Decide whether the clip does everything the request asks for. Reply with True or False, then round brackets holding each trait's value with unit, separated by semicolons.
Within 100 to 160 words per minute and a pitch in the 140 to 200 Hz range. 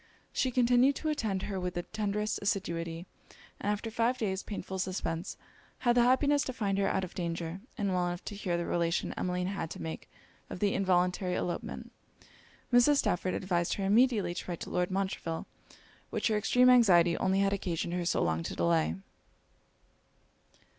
False (175 wpm; 190 Hz)